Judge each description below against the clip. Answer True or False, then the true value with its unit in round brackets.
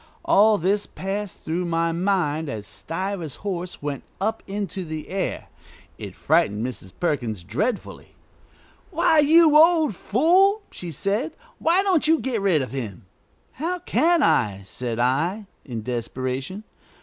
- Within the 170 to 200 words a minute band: False (135 wpm)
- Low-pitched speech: False (185 Hz)